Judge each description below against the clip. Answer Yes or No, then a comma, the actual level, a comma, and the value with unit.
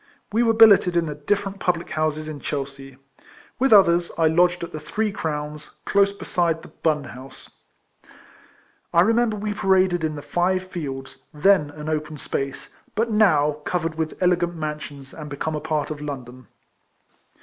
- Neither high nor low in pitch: Yes, medium, 160 Hz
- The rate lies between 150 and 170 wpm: Yes, average, 160 wpm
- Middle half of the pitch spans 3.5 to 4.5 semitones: Yes, average, 4.0 semitones